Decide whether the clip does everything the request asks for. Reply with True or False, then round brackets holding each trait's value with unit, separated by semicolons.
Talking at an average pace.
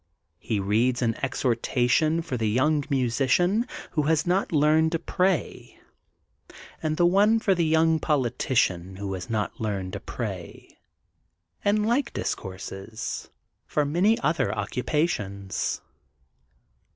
False (125 wpm)